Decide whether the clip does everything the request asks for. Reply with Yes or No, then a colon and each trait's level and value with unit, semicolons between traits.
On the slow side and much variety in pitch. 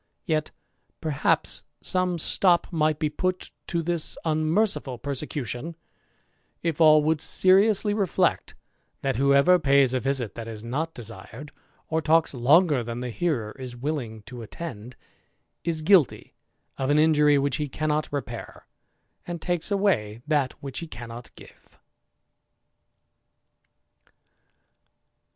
No: slow, 120 wpm; average, 4.8 semitones